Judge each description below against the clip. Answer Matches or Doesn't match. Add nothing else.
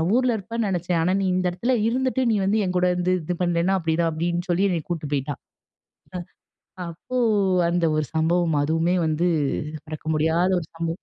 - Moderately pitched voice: Matches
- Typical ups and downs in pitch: Doesn't match